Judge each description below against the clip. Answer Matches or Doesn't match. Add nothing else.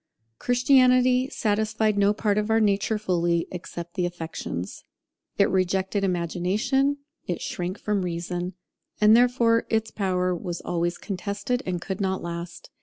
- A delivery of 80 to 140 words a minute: Matches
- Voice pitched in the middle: Doesn't match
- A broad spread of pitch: Doesn't match